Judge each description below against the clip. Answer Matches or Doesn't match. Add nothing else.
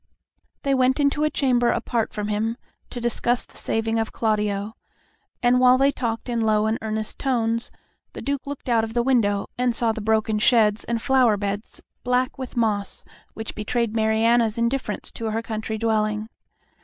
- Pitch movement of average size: Doesn't match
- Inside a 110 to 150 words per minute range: Doesn't match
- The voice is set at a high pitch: Matches